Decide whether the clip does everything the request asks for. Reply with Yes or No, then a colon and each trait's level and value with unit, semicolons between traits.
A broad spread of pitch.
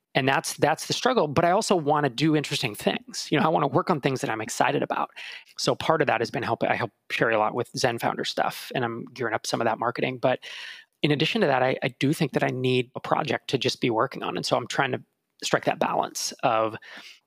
No: average, 3.4 semitones